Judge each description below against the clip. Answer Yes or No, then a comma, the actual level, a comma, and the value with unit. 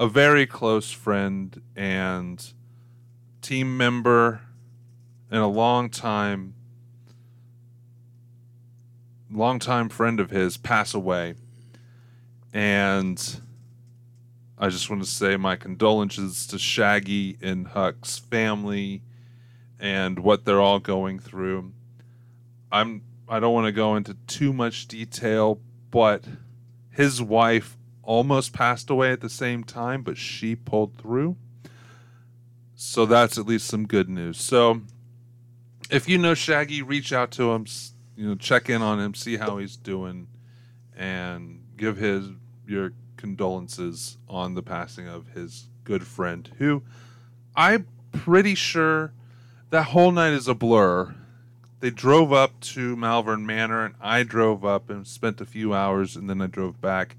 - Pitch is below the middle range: Yes, low, 120 Hz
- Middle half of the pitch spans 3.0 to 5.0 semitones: No, narrow, 2.6 semitones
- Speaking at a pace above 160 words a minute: No, slow, 135 wpm